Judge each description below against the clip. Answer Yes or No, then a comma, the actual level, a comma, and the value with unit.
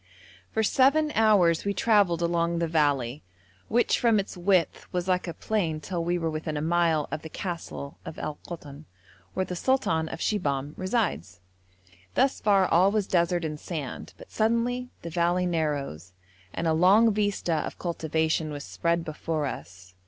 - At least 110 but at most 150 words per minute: No, average, 165 wpm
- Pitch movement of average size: Yes, average, 4.3 semitones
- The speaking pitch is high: No, medium, 170 Hz